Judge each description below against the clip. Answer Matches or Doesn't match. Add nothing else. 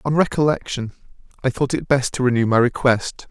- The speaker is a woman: Doesn't match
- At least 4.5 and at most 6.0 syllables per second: Matches